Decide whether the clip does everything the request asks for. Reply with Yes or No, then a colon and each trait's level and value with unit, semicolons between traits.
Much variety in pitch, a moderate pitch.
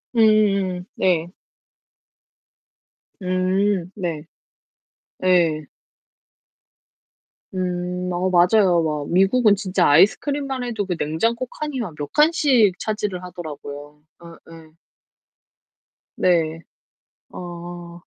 No: average, 3.5 semitones; medium, 180 Hz